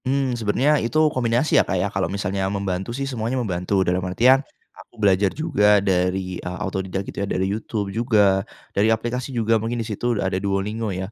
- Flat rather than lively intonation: No, average, 3.7 semitones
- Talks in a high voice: No, low, 105 Hz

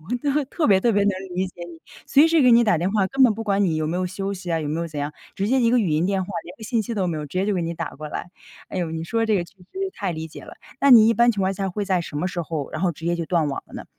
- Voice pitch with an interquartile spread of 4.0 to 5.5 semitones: Yes, average, 4.6 semitones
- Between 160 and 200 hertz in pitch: Yes, high, 190 Hz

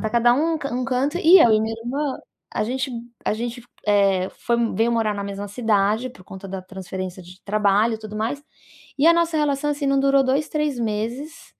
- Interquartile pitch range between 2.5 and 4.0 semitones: No, average, 5.2 semitones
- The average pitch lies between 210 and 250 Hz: Yes, high, 235 Hz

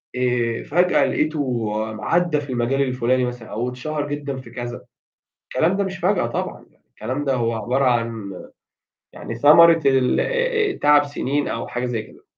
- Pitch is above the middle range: No, low, 135 Hz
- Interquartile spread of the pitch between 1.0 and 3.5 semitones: No, average, 3.9 semitones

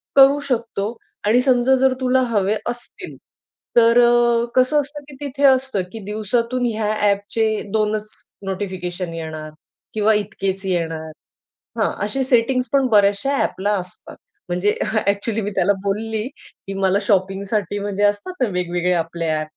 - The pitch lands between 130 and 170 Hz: No, high, 210 Hz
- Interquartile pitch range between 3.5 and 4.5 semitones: Yes, average, 3.9 semitones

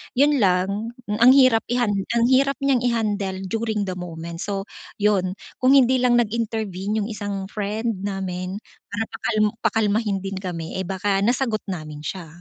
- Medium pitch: No, high, 205 Hz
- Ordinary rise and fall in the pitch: Yes, average, 3.3 semitones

